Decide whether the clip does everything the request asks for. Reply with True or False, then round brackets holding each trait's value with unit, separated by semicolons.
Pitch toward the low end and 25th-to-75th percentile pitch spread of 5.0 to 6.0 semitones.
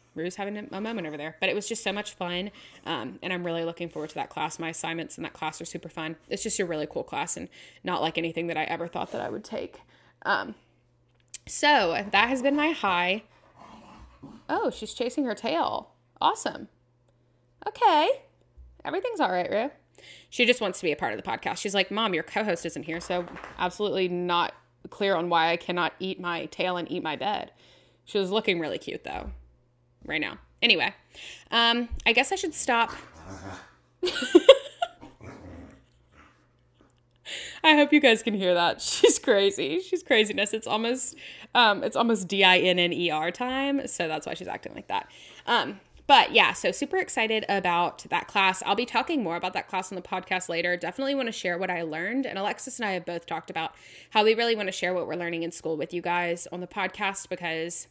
False (190 Hz; 5.4 semitones)